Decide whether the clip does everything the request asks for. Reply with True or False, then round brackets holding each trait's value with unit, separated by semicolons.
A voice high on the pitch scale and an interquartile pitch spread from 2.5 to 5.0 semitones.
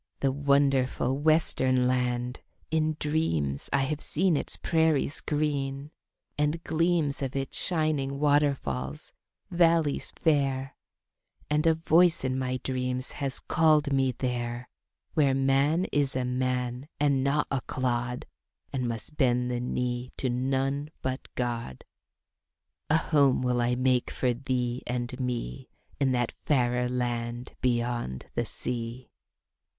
False (130 Hz; 2.9 semitones)